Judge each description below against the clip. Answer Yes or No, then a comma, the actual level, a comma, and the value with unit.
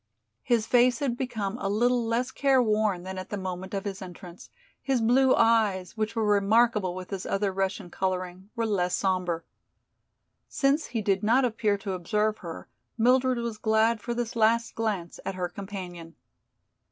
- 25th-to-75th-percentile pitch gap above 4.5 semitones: No, average, 3.7 semitones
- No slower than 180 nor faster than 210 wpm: No, average, 165 wpm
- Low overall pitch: No, high, 210 Hz